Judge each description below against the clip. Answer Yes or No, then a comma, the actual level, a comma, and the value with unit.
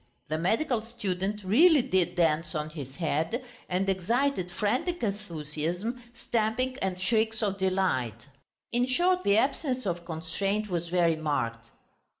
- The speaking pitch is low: No, high, 195 Hz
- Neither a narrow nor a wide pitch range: No, wide, 5.9 semitones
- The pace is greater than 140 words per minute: No, slow, 135 wpm